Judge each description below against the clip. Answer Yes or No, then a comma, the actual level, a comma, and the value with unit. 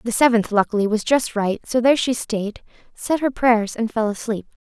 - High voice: Yes, high, 230 Hz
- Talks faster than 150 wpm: Yes, fast, 205 wpm